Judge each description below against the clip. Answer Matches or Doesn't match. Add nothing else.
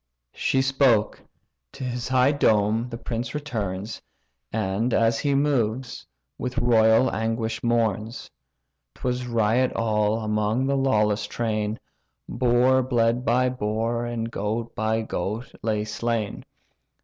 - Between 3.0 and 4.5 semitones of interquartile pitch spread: Doesn't match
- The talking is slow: Matches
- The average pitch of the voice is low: Matches